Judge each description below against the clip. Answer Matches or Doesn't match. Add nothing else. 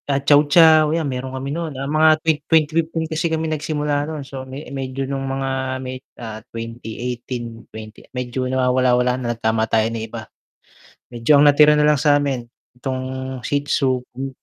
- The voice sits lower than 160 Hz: Matches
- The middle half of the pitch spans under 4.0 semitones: Matches